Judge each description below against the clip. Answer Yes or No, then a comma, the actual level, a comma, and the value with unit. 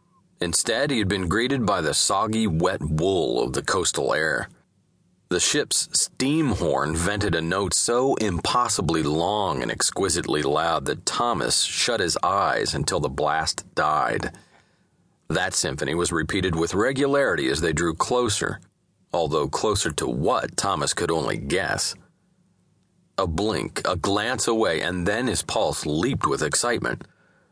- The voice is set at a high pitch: No, very low, 95 Hz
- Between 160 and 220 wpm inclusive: No, average, 145 wpm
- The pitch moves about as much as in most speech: No, wide, 6.9 semitones